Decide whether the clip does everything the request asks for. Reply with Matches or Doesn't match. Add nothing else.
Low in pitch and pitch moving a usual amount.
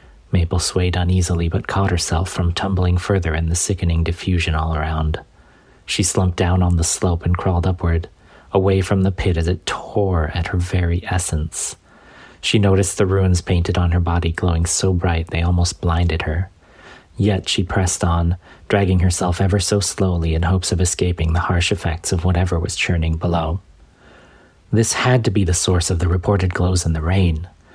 Doesn't match